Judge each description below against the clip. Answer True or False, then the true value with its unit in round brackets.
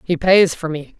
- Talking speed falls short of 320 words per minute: True (240 wpm)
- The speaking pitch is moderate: True (165 Hz)